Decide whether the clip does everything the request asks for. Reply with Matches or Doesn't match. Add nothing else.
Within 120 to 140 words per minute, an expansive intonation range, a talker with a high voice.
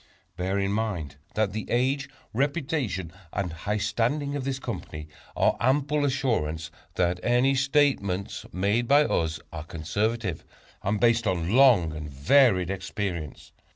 Doesn't match